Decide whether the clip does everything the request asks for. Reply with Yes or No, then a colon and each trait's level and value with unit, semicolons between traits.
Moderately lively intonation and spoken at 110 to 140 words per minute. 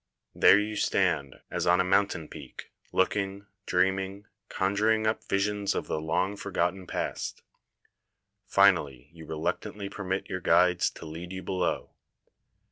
No: narrow, 2.3 semitones; slow, 135 wpm